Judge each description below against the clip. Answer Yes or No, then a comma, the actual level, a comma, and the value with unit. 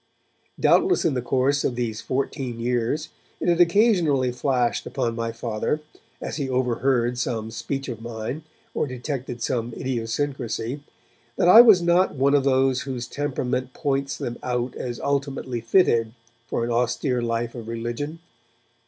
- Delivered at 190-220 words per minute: No, average, 150 wpm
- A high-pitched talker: No, low, 130 Hz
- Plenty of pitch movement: No, average, 3.2 semitones